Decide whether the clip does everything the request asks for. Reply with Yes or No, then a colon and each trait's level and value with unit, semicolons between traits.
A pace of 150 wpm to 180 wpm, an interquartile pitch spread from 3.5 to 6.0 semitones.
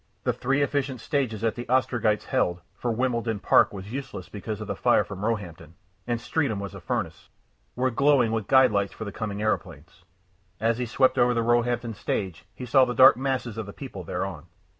No: average, 200 wpm; average, 3.9 semitones